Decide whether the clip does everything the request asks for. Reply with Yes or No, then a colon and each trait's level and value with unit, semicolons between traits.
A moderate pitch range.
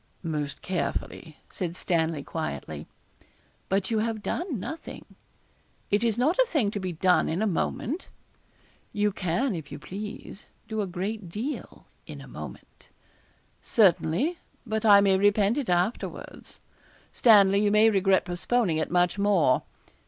Yes: average, 3.7 semitones